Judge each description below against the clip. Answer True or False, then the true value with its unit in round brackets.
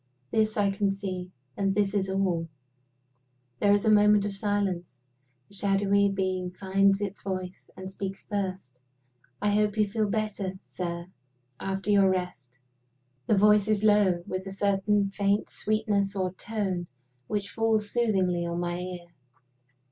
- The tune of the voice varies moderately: False (1.8 semitones)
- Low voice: False (195 Hz)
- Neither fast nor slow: True (150 wpm)